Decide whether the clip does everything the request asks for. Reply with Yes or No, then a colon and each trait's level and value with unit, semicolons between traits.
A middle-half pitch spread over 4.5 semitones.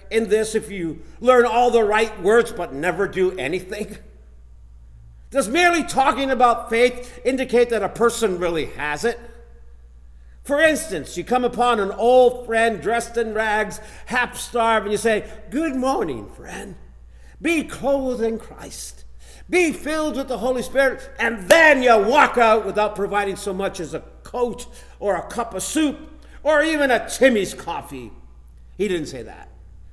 Yes: average, 5.2 semitones